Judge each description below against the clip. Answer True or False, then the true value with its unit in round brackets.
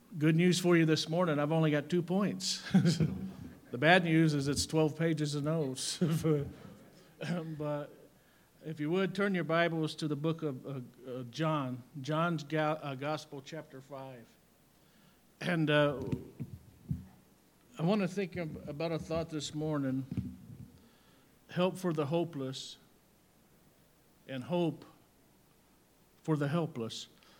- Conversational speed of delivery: False (125 wpm)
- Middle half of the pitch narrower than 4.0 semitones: True (3.0 semitones)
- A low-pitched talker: False (155 Hz)